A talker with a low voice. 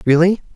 No: medium, 175 Hz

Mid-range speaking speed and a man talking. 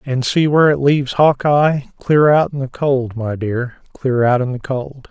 No: fast, 210 wpm; male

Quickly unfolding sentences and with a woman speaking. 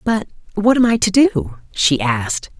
No: average, 185 wpm; female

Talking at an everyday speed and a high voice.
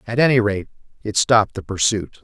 No: average, 190 wpm; low, 105 Hz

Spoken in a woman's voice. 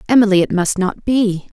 Yes: female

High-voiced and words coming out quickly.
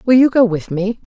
Yes: high, 215 Hz; fast, 270 wpm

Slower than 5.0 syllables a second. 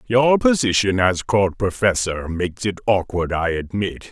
Yes: 4.4 syllables/s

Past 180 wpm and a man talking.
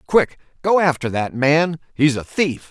No: slow, 135 wpm; male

